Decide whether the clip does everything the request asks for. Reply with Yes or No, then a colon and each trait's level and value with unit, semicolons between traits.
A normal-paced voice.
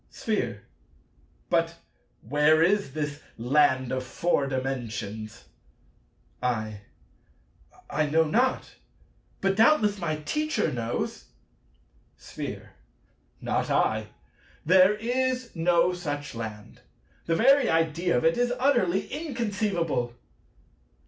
No: slow, 95 wpm